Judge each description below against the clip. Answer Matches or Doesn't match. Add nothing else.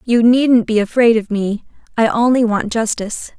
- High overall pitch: Matches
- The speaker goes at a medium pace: Matches